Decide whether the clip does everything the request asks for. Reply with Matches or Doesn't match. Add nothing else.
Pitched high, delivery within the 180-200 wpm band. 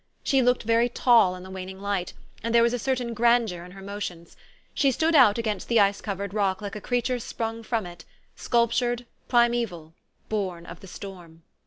Matches